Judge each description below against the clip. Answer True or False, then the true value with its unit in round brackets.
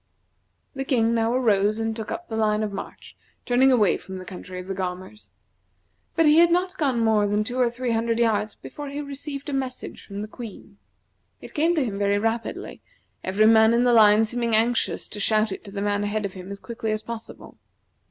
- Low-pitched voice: False (225 Hz)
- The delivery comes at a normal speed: False (215 wpm)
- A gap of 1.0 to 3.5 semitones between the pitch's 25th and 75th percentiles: True (3.2 semitones)